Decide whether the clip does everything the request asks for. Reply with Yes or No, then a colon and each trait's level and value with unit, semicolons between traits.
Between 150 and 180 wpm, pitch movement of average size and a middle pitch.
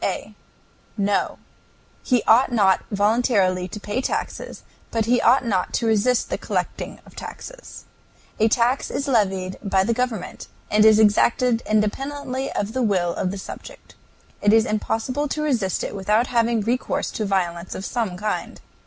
No: average, 160 wpm; average, 3.7 semitones; high, 220 Hz